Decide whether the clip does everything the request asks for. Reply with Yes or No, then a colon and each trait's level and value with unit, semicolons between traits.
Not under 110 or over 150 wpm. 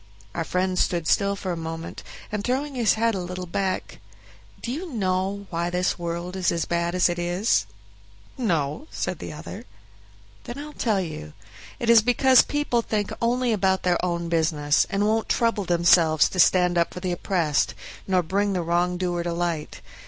No: average, 180 wpm